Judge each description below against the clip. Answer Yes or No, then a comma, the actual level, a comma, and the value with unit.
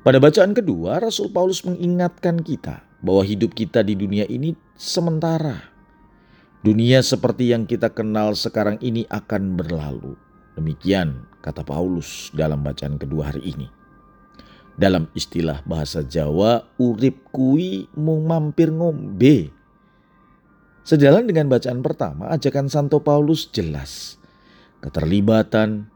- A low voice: Yes, low, 115 Hz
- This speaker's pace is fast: No, average, 115 wpm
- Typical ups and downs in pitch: No, wide, 8.5 semitones